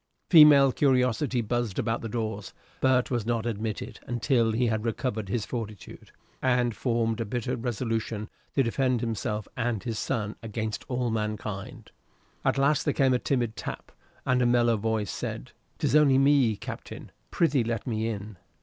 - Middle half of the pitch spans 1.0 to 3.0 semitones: Yes, narrow, 2.5 semitones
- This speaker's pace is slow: No, average, 165 wpm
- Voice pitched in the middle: No, low, 115 Hz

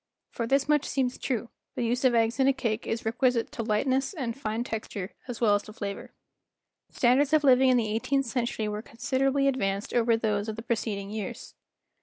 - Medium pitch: No, high, 235 Hz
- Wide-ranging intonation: No, average, 3.2 semitones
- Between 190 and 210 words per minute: Yes, average, 200 wpm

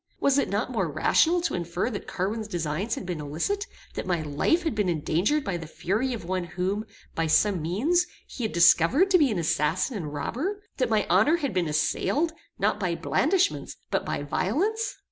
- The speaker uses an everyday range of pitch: No, wide, 8.8 semitones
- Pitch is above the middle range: Yes, high, 205 Hz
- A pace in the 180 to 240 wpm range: Yes, average, 195 wpm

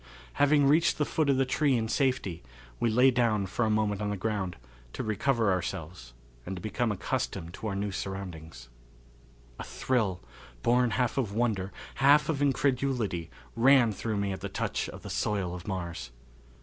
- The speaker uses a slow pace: No, average, 175 wpm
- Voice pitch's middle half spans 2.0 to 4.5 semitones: No, average, 5.3 semitones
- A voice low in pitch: Yes, low, 110 Hz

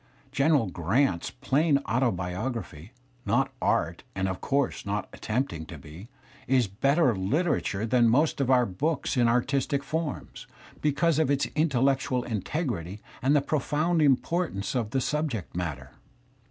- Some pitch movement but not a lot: No, wide, 6.4 semitones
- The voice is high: No, low, 125 Hz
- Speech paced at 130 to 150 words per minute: Yes, average, 145 wpm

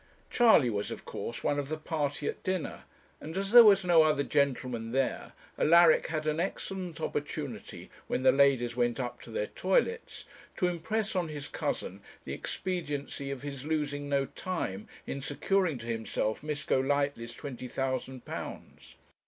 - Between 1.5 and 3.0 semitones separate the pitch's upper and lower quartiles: No, average, 4.7 semitones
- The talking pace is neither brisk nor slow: Yes, average, 160 wpm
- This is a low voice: No, medium, 145 Hz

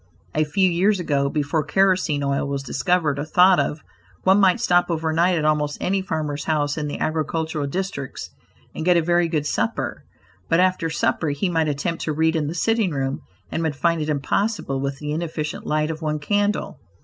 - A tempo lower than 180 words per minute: No, average, 195 wpm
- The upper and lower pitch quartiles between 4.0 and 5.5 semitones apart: No, average, 3.2 semitones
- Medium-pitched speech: Yes, medium, 160 Hz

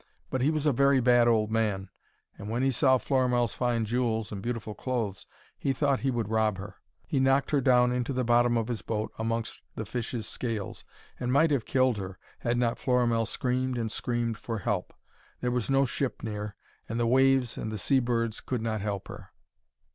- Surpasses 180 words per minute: Yes, average, 200 wpm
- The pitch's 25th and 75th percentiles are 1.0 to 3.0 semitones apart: Yes, narrow, 2.6 semitones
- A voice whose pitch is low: Yes, low, 120 Hz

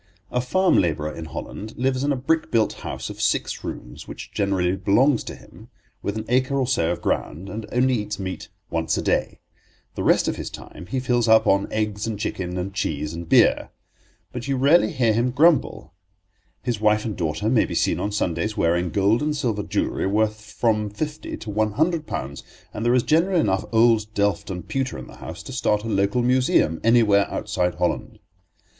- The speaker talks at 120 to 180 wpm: No, average, 200 wpm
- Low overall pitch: Yes, low, 110 Hz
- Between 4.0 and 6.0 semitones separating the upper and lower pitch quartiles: Yes, average, 4.6 semitones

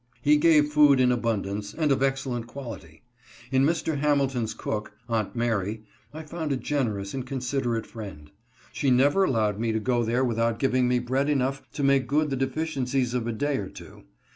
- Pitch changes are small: No, average, 3.6 semitones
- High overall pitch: No, low, 130 Hz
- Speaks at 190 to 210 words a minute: Yes, average, 195 wpm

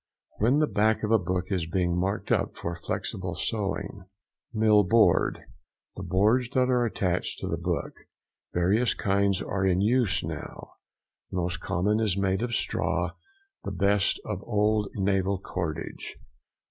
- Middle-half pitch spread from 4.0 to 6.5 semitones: No, average, 2.8 semitones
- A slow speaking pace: No, average, 145 wpm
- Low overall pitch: Yes, low, 100 Hz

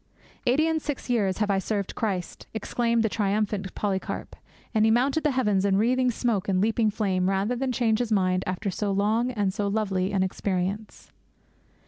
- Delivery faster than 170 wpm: Yes, average, 180 wpm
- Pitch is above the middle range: Yes, high, 210 Hz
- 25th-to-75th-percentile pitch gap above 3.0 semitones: Yes, average, 3.4 semitones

